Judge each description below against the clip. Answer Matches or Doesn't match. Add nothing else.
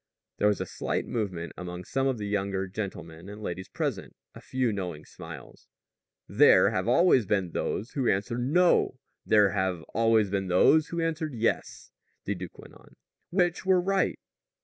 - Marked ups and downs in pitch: Matches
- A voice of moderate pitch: Doesn't match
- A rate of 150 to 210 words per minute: Matches